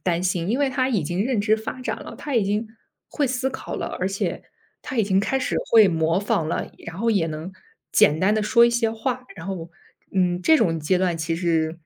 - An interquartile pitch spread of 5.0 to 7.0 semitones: Yes, wide, 5.5 semitones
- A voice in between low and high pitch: No, high, 195 Hz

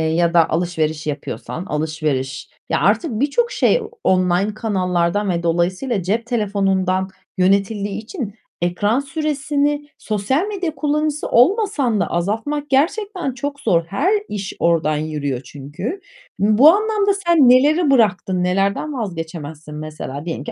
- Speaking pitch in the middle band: No, high, 205 Hz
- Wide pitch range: Yes, wide, 8.9 semitones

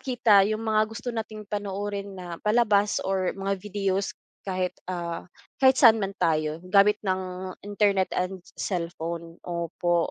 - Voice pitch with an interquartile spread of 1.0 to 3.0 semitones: Yes, narrow, 2.5 semitones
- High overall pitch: Yes, high, 195 Hz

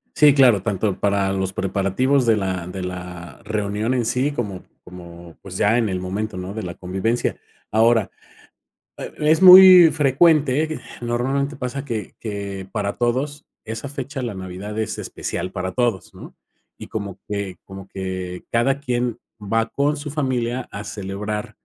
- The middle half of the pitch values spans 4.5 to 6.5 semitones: Yes, average, 5.2 semitones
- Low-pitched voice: Yes, low, 110 Hz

